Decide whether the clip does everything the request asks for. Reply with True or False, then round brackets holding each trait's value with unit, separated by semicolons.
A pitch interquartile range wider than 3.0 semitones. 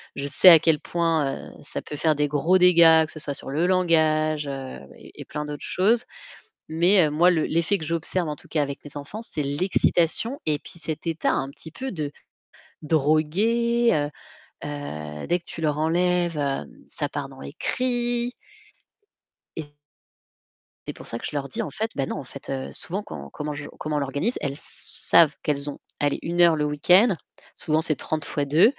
True (3.4 semitones)